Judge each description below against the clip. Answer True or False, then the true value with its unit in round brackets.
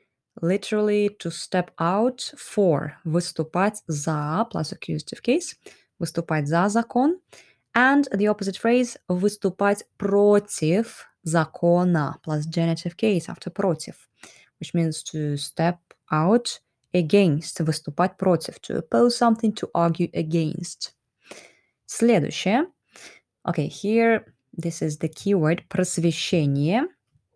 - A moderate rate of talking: False (105 wpm)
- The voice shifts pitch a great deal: False (4.4 semitones)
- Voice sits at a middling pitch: True (180 Hz)